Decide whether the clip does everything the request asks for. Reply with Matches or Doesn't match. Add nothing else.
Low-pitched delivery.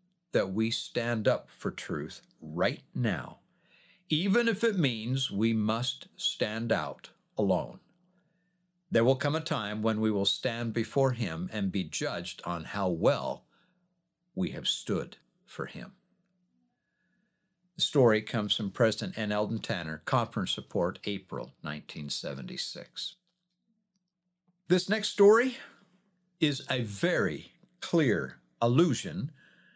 Doesn't match